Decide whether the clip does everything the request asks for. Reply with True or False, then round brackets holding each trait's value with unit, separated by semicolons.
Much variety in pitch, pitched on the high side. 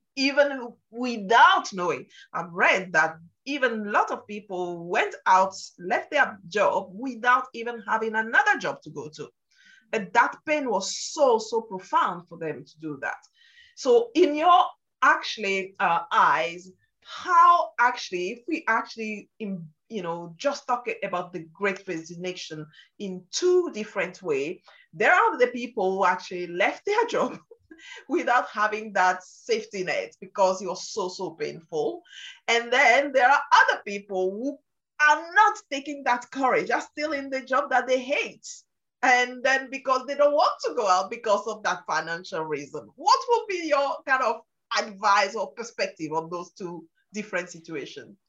True (7.4 semitones; 225 Hz)